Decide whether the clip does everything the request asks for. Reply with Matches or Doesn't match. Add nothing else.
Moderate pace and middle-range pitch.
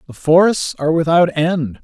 Matches